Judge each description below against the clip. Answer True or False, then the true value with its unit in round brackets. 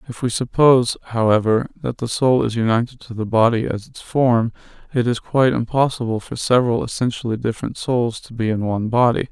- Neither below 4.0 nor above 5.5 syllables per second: False (5.9 syllables/s)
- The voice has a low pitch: True (120 Hz)